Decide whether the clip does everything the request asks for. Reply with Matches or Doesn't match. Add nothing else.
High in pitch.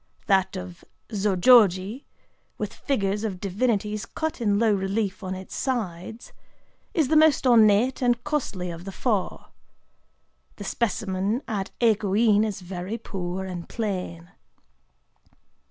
Matches